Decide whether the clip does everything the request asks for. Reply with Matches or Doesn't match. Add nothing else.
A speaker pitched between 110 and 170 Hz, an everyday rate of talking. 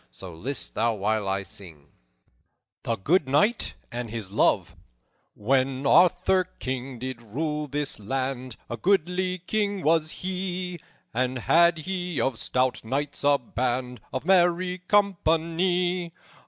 Doesn't match